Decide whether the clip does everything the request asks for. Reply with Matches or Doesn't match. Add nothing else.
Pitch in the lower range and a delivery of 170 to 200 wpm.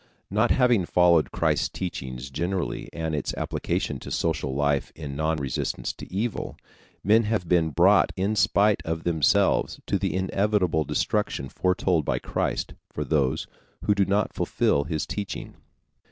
Doesn't match